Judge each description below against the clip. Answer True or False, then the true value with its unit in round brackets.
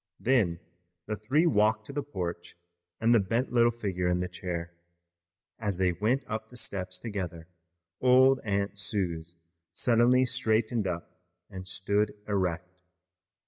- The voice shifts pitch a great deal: False (4.5 semitones)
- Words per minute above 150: False (140 wpm)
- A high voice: False (105 Hz)